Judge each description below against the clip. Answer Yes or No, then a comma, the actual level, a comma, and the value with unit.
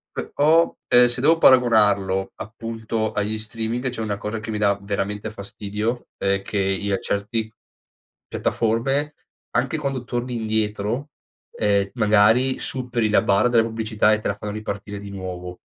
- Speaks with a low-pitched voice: Yes, low, 110 Hz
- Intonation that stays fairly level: No, average, 3.0 semitones